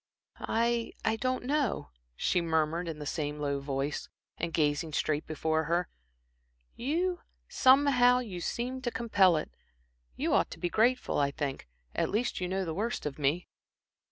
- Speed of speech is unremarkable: Yes, average, 160 wpm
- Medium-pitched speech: Yes, medium, 180 Hz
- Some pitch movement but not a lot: No, wide, 8.0 semitones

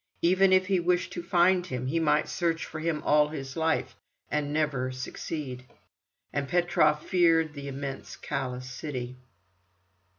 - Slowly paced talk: No, average, 145 wpm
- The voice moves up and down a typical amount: Yes, average, 4.0 semitones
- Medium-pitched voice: Yes, medium, 150 Hz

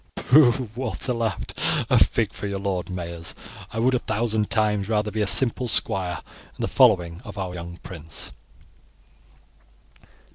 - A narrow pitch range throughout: No, average, 4.3 semitones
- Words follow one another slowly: No, average, 150 wpm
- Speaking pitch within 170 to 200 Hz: No, low, 105 Hz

